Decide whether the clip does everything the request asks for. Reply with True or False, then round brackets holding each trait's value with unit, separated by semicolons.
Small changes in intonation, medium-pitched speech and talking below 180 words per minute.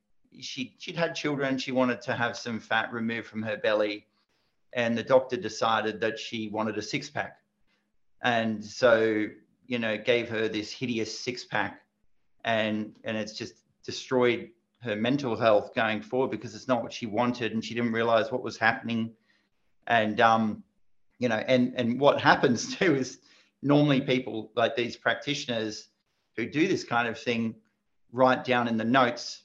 False (2.3 semitones; 115 Hz; 170 wpm)